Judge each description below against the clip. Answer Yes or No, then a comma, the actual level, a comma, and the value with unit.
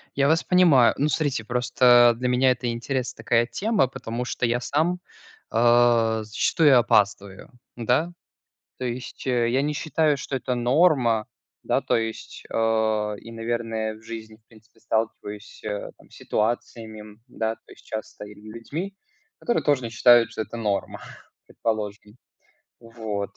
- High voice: No, low, 120 Hz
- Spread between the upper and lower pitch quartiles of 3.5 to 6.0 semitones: No, average, 2.7 semitones